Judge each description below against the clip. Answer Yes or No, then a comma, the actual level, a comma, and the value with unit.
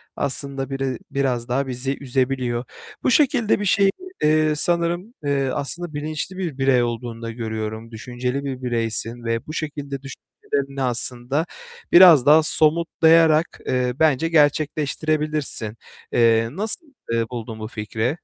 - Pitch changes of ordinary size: Yes, average, 4.3 semitones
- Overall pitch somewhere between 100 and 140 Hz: Yes, low, 135 Hz